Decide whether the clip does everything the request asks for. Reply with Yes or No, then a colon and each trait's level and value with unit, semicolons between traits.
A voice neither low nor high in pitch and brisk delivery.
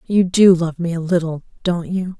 Yes: medium, 175 Hz; fast, 220 wpm